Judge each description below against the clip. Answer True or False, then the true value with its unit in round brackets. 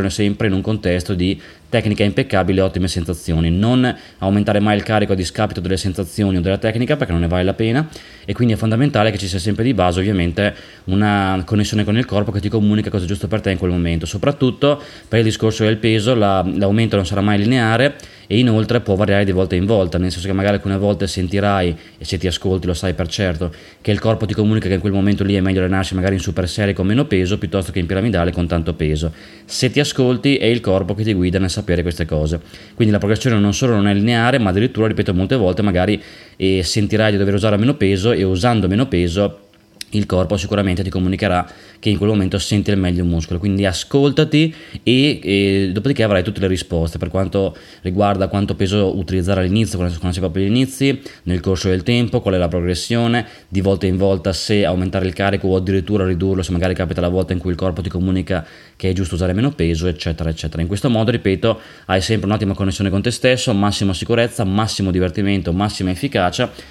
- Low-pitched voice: True (100 Hz)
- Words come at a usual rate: False (220 wpm)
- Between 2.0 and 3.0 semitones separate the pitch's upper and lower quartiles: True (2.7 semitones)